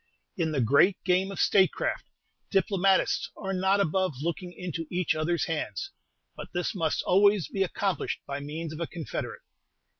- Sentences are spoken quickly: No, average, 155 wpm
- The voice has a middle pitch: Yes, medium, 180 Hz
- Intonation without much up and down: No, average, 3.2 semitones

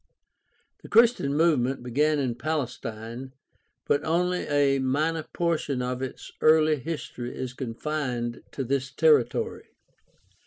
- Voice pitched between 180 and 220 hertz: No, medium, 140 Hz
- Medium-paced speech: No, slow, 125 wpm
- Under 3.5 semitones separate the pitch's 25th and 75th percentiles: No, average, 3.8 semitones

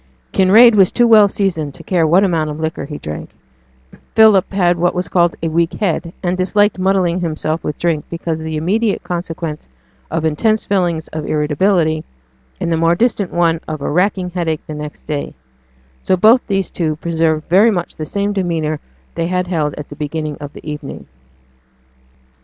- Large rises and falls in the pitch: No, average, 3.3 semitones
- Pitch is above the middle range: No, medium, 170 Hz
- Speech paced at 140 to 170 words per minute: No, average, 180 wpm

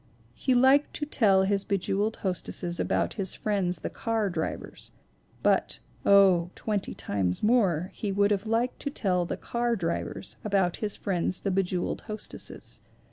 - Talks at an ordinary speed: Yes, average, 160 wpm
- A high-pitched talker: Yes, high, 200 Hz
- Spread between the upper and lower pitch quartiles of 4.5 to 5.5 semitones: No, average, 3.4 semitones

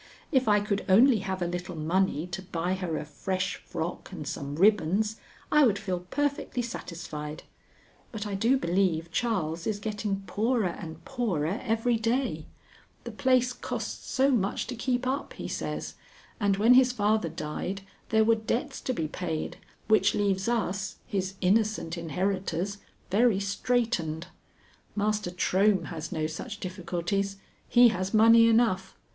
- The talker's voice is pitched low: No, high, 200 Hz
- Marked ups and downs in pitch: No, average, 4.2 semitones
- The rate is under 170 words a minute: Yes, average, 150 wpm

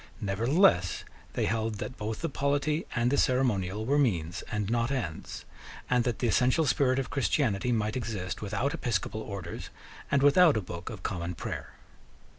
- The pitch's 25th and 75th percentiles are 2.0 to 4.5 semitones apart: No, wide, 5.4 semitones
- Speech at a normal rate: Yes, average, 165 wpm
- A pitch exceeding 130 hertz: No, low, 115 Hz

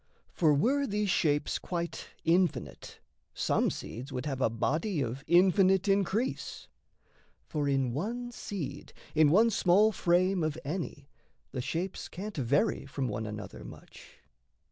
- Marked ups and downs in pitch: Yes, wide, 5.8 semitones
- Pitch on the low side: No, medium, 170 Hz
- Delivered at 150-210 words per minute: No, slow, 135 wpm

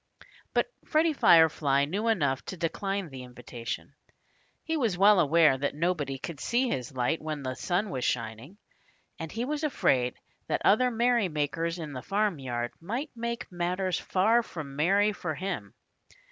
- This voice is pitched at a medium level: Yes, medium, 170 Hz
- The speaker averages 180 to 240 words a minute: No, average, 155 wpm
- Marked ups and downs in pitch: Yes, wide, 7.2 semitones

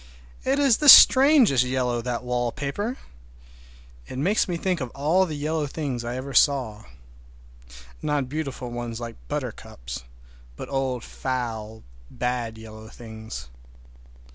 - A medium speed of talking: No, slow, 120 wpm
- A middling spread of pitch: Yes, average, 4.9 semitones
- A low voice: Yes, low, 125 Hz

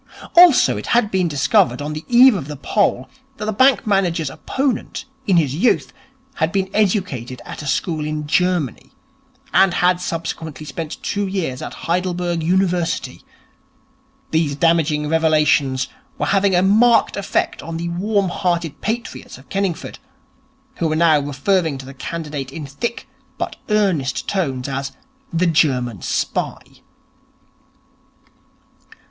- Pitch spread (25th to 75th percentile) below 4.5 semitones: No, average, 4.8 semitones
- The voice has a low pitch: No, medium, 165 Hz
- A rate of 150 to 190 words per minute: No, average, 140 wpm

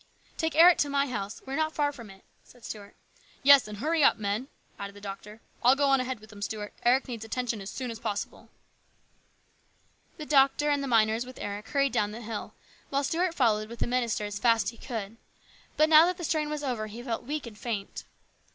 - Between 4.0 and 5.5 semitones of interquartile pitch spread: Yes, average, 4.8 semitones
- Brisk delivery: Yes, fast, 235 wpm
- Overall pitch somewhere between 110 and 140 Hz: No, high, 240 Hz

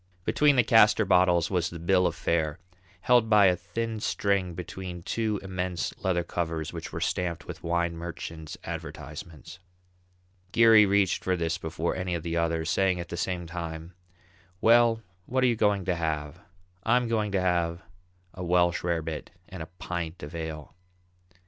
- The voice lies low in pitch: Yes, very low, 90 Hz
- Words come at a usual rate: Yes, average, 165 wpm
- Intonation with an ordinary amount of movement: Yes, average, 3.0 semitones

